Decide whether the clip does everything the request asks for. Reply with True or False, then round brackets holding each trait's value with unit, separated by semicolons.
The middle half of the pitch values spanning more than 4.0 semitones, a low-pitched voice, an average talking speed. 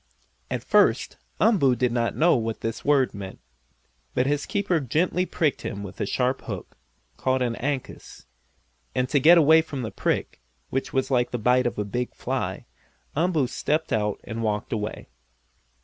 True (4.8 semitones; 130 Hz; 170 wpm)